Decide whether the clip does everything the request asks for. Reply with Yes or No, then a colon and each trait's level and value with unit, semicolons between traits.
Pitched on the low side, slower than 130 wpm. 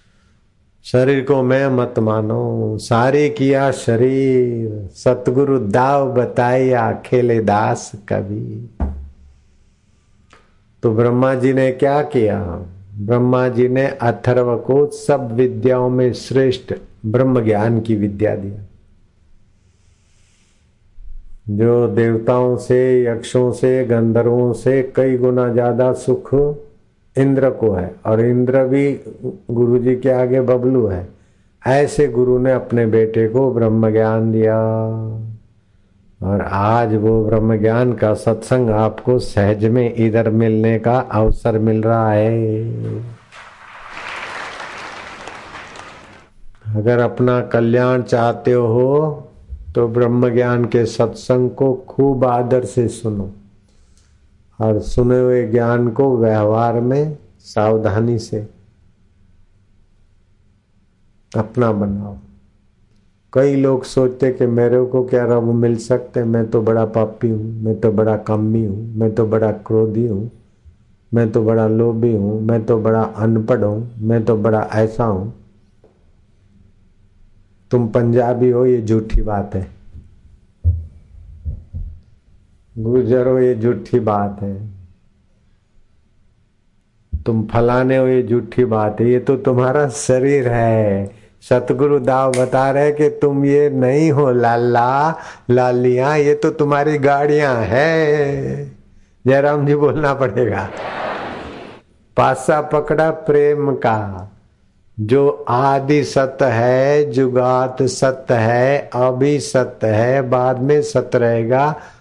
Yes: low, 115 Hz; slow, 110 wpm